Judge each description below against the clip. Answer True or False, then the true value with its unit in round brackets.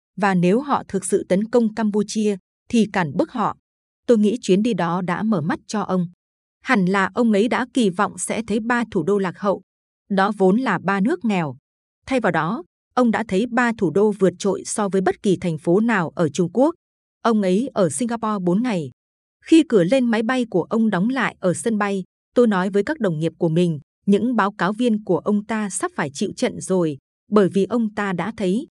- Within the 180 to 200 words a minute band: False (225 wpm)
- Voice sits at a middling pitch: False (205 Hz)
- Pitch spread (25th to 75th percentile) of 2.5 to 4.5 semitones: True (3.7 semitones)